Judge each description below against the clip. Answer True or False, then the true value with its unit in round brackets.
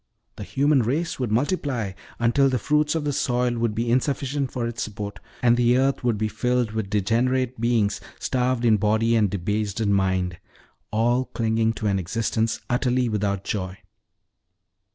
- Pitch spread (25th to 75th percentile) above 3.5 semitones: False (3.2 semitones)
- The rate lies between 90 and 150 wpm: False (160 wpm)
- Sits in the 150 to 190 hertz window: False (115 Hz)